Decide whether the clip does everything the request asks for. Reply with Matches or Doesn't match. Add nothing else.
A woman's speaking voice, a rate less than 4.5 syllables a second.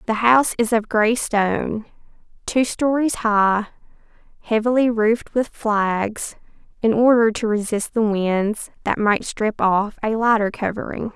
Matches